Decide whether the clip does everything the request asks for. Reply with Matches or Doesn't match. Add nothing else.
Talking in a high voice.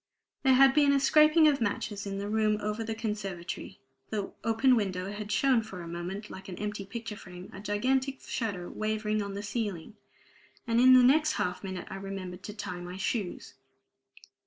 Matches